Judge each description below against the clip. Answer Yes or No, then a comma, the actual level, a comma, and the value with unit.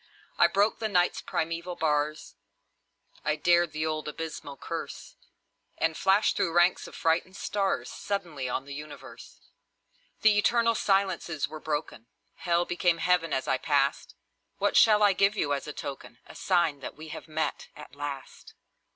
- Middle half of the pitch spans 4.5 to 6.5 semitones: No, average, 3.9 semitones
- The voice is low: No, medium, 165 Hz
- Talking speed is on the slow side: No, average, 160 wpm